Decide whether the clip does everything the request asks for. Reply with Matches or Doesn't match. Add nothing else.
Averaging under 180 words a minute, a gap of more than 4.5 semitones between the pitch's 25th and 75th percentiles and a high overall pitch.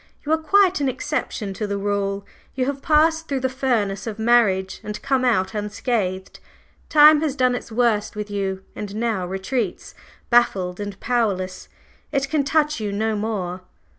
Matches